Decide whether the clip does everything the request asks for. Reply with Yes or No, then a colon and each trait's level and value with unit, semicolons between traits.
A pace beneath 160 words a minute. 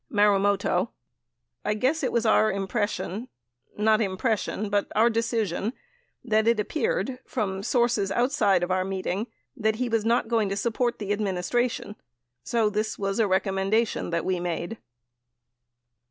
Yes: average, 145 wpm